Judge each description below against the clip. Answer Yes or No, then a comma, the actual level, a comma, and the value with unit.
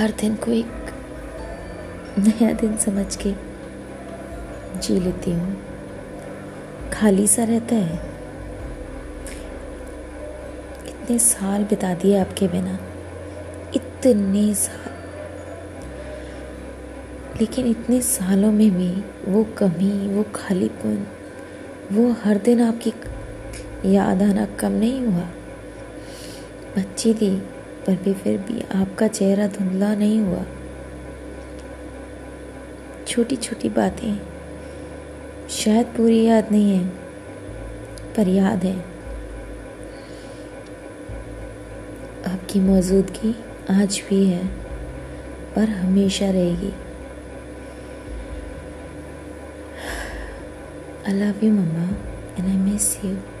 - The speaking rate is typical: No, slow, 85 wpm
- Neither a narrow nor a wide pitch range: Yes, average, 3.4 semitones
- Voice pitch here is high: Yes, high, 195 Hz